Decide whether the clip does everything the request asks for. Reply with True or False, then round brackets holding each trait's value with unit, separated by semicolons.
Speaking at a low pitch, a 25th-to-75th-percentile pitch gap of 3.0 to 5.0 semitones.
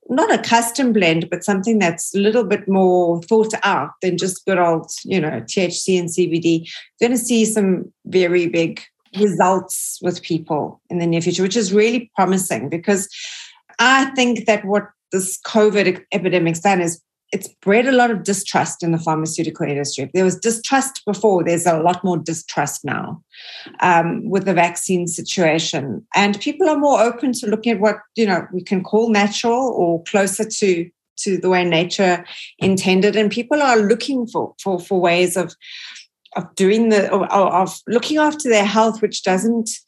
False (190 Hz; 3.9 semitones)